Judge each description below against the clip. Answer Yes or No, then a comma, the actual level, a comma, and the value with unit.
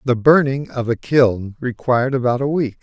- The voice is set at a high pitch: No, low, 125 Hz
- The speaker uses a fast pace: No, average, 190 wpm